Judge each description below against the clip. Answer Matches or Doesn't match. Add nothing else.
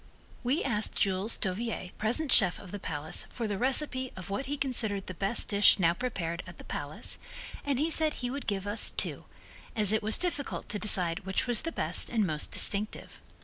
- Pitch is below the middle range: Doesn't match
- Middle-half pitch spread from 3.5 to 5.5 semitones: Matches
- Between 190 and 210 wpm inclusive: Matches